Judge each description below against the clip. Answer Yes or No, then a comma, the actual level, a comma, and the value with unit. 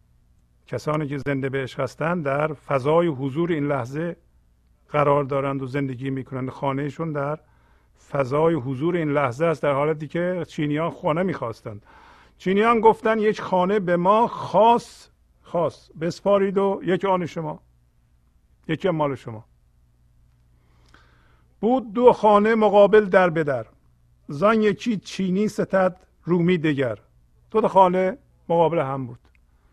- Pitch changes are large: Yes, wide, 7.8 semitones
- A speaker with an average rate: Yes, average, 130 wpm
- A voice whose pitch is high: No, medium, 150 Hz